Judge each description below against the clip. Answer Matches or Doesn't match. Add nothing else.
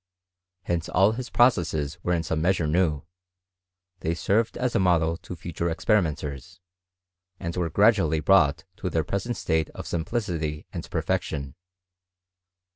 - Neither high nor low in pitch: Doesn't match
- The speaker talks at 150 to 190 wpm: Doesn't match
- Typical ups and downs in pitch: Matches